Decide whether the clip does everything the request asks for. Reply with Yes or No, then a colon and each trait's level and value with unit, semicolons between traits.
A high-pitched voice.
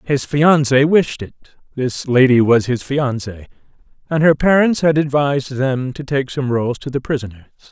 No: low, 135 Hz